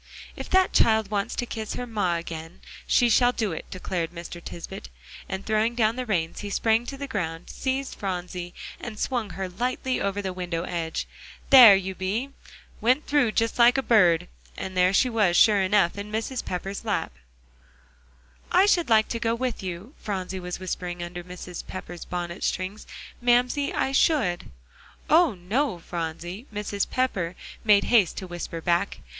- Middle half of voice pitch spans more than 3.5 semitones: Yes, average, 5.1 semitones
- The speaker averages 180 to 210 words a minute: No, average, 170 wpm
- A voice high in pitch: Yes, high, 200 Hz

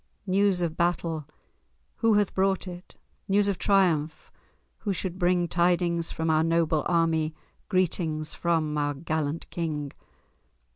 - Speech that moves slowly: Yes, slow, 130 wpm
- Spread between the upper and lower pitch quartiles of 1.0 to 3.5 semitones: Yes, average, 2.7 semitones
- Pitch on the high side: No, medium, 170 Hz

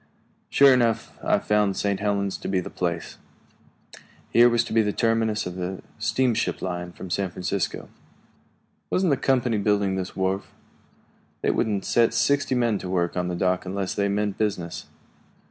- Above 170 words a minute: No, average, 165 wpm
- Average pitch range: Yes, average, 3.6 semitones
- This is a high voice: No, low, 100 Hz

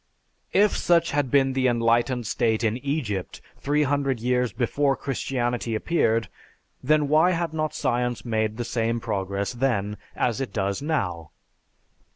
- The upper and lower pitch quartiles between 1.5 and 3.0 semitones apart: No, average, 4.2 semitones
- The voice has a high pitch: No, low, 125 Hz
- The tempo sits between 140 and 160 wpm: Yes, average, 145 wpm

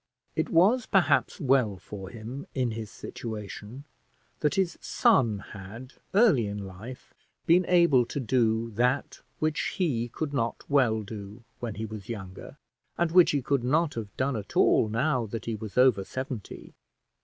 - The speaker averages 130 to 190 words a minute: Yes, average, 160 wpm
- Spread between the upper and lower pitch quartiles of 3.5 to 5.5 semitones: Yes, average, 4.7 semitones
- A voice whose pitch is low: Yes, low, 120 Hz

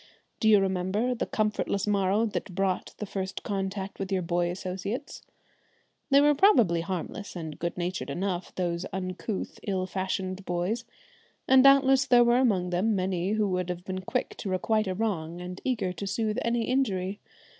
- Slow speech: No, average, 170 wpm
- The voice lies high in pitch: Yes, high, 195 Hz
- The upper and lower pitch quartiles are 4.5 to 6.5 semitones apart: No, average, 3.3 semitones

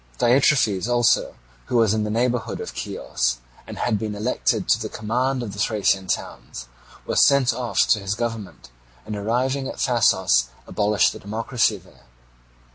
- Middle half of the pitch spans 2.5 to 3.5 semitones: Yes, average, 3.2 semitones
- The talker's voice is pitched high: No, low, 110 Hz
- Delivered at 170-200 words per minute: No, average, 160 wpm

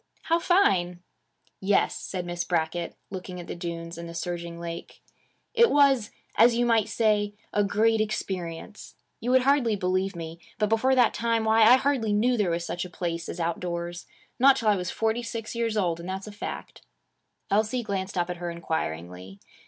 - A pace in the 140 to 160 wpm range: No, average, 185 wpm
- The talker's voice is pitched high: Yes, high, 195 Hz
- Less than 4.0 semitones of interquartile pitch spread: No, average, 4.8 semitones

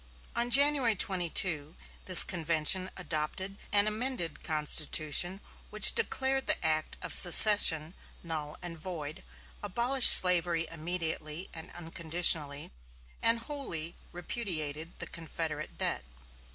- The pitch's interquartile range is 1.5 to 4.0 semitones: No, average, 4.4 semitones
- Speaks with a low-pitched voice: No, medium, 170 Hz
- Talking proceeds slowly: Yes, slow, 105 wpm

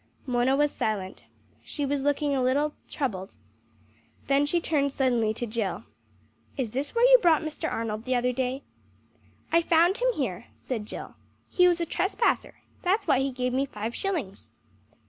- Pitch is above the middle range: Yes, very high, 275 Hz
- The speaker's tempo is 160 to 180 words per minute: Yes, average, 165 wpm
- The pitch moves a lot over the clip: No, average, 4.8 semitones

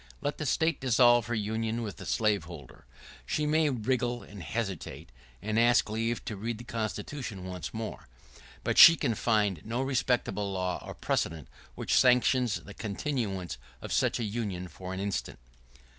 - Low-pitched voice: Yes, low, 110 Hz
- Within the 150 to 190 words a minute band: Yes, average, 160 wpm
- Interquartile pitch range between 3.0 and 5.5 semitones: Yes, average, 3.8 semitones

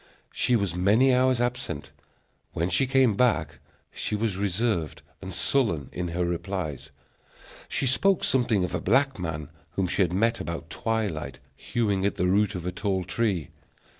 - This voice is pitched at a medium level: No, low, 100 Hz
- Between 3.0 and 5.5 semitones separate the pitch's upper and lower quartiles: Yes, average, 5.2 semitones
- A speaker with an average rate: Yes, average, 165 wpm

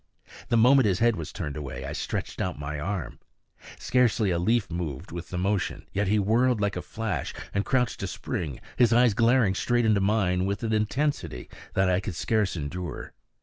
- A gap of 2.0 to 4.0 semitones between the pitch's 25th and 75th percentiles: No, average, 4.4 semitones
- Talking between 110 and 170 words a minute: No, average, 190 wpm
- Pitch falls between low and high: No, low, 100 Hz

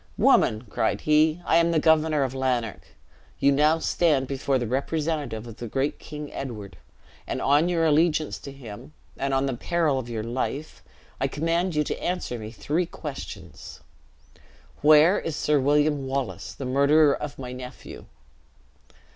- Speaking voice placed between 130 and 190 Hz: Yes, medium, 140 Hz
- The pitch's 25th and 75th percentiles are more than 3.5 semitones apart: No, average, 3.2 semitones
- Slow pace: No, average, 160 wpm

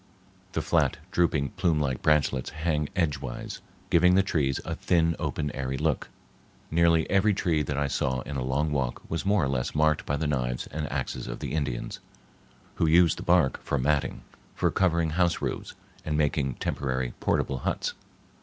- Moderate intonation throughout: Yes, average, 3.7 semitones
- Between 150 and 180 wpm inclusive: Yes, average, 175 wpm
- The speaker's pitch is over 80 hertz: No, very low, 75 Hz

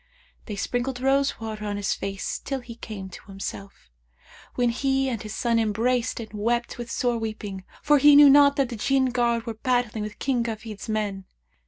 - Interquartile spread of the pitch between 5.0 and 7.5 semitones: No, average, 3.2 semitones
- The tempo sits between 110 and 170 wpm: No, average, 190 wpm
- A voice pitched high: Yes, high, 235 Hz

